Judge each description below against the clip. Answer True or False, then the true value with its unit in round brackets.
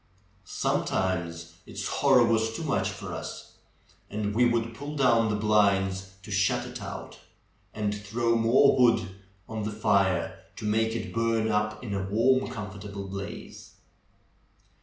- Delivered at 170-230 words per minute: False (145 wpm)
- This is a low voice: True (105 Hz)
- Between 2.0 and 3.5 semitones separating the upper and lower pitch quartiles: True (2.6 semitones)